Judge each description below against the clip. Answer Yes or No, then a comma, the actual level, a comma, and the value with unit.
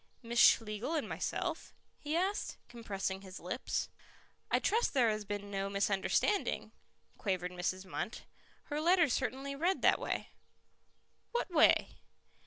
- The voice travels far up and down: Yes, wide, 7.7 semitones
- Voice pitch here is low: No, high, 230 Hz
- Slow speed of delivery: Yes, slow, 130 wpm